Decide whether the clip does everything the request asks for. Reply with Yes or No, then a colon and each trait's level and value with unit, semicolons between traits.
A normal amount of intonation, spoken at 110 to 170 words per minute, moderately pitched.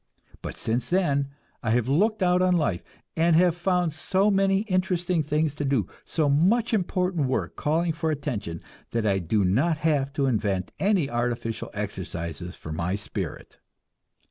No: wide, 8.0 semitones; average, 160 wpm; medium, 150 Hz